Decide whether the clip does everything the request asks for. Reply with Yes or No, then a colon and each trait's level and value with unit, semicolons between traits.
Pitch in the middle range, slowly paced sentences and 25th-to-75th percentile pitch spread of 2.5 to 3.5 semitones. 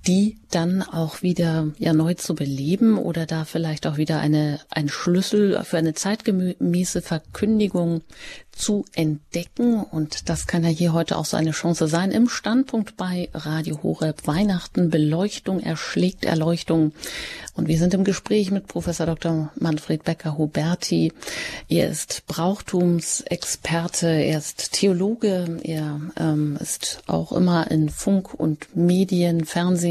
No: medium, 170 Hz; average, 140 wpm; average, 2.9 semitones